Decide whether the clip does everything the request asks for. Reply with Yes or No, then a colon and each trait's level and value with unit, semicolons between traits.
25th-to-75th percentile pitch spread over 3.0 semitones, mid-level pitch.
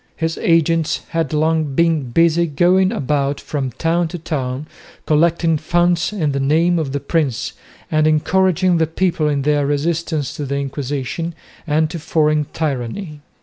No: average, 2.7 semitones; medium, 155 Hz